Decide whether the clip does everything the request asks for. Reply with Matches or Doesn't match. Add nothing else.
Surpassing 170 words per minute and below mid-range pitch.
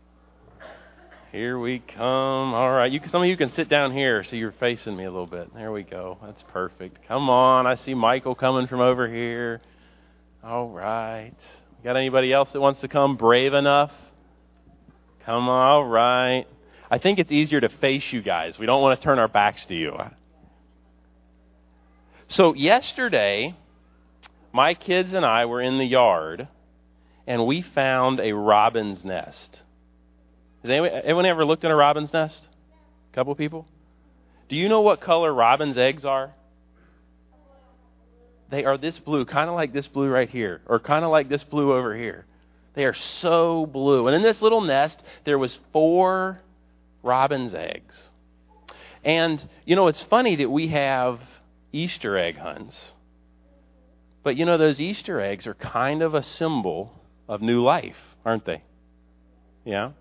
Doesn't match